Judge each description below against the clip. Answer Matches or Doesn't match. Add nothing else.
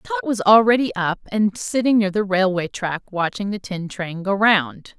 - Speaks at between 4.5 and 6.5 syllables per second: Doesn't match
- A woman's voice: Matches